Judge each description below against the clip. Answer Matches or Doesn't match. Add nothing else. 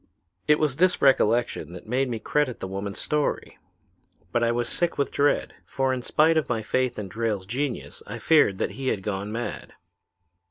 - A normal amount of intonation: Matches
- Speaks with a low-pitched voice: Matches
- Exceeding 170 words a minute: Matches